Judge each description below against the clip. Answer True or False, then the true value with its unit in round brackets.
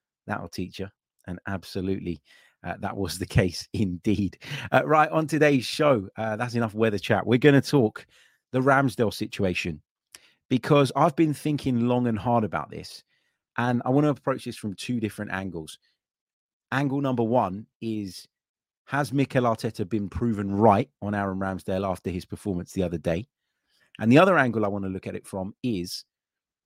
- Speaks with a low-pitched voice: True (110 Hz)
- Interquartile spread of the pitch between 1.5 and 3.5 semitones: False (5.1 semitones)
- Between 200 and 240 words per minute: False (175 wpm)